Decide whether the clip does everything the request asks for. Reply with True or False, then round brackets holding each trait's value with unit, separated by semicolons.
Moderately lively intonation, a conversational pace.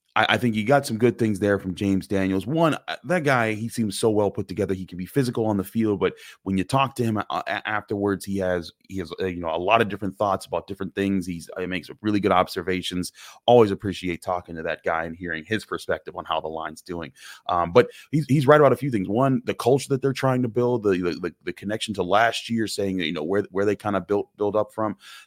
False (3.9 semitones; 250 wpm)